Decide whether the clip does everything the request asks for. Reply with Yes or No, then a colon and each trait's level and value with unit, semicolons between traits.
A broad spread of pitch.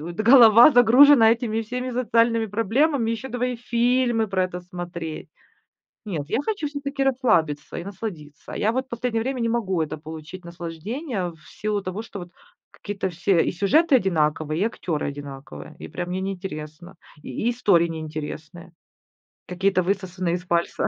Yes: wide, 5.7 semitones